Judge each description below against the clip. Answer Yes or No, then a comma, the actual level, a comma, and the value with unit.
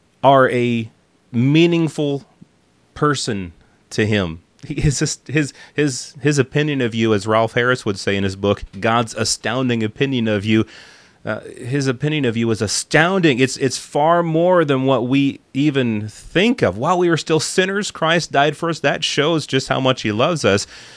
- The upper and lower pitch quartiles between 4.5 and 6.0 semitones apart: Yes, average, 5.2 semitones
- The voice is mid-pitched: No, low, 130 Hz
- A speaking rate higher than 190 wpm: No, average, 175 wpm